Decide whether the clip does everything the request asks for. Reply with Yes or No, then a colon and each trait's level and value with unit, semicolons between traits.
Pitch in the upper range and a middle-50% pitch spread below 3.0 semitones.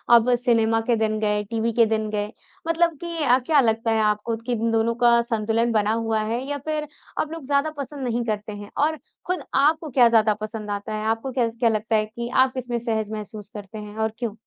Yes: high, 225 Hz; narrow, 2.6 semitones